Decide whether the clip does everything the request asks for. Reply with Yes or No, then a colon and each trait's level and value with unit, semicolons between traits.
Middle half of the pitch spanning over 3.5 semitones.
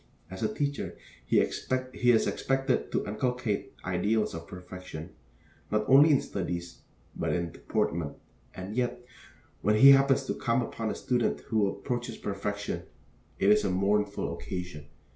Yes: average, 5.0 semitones